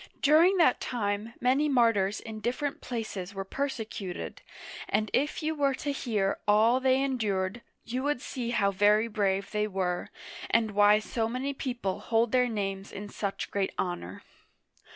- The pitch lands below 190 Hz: No, high, 225 Hz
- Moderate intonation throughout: Yes, average, 4.3 semitones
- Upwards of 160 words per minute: No, average, 155 wpm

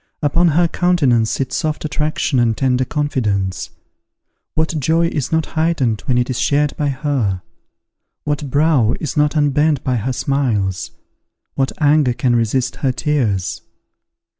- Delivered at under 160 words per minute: Yes, average, 140 wpm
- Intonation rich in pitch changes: No, average, 4.0 semitones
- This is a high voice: No, medium, 140 Hz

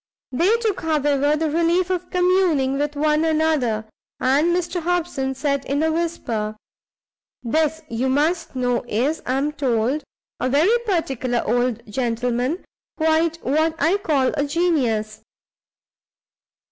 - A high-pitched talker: Yes, very high, 295 Hz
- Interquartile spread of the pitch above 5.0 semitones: No, average, 4.5 semitones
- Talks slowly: Yes, slow, 130 wpm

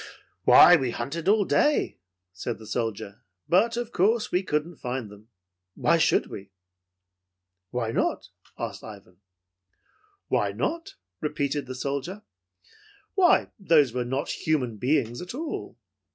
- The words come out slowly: Yes, slow, 130 wpm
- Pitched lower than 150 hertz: Yes, medium, 140 Hz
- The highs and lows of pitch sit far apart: Yes, wide, 7.9 semitones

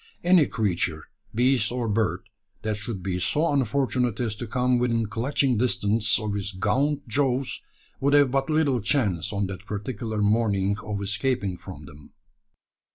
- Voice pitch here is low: Yes, low, 110 Hz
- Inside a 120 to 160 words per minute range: Yes, average, 155 wpm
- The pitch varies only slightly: No, average, 4.3 semitones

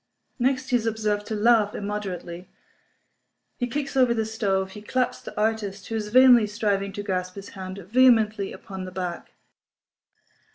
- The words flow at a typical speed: Yes, average, 160 wpm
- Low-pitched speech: No, high, 210 Hz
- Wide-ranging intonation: No, average, 3.1 semitones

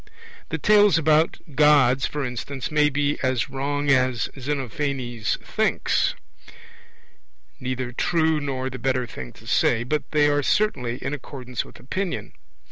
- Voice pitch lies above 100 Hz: Yes, medium, 140 Hz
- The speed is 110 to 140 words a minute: Yes, slow, 135 wpm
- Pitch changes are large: No, average, 2.8 semitones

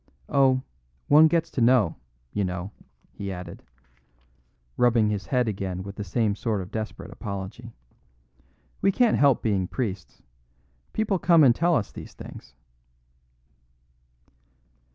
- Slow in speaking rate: Yes, slow, 130 wpm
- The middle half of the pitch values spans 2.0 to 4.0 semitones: No, wide, 5.6 semitones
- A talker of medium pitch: No, low, 110 Hz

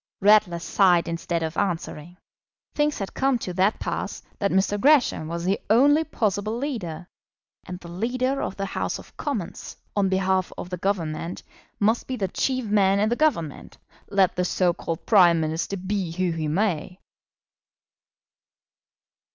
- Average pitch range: Yes, average, 3.9 semitones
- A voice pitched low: No, high, 190 Hz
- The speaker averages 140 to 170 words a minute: Yes, average, 155 wpm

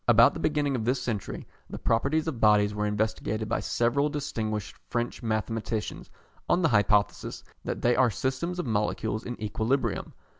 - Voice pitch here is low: Yes, low, 115 Hz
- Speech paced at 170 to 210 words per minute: No, average, 160 wpm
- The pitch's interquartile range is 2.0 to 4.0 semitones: Yes, average, 3.6 semitones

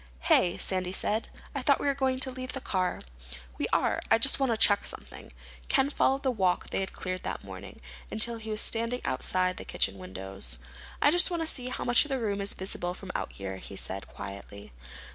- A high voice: Yes, high, 205 Hz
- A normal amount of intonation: No, wide, 6.4 semitones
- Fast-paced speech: Yes, fast, 220 wpm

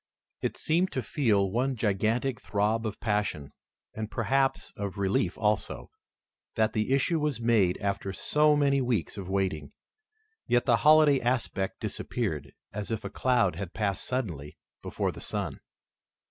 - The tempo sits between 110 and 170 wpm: Yes, average, 145 wpm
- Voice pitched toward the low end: Yes, low, 110 Hz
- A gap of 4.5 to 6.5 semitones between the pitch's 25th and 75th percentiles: Yes, average, 4.8 semitones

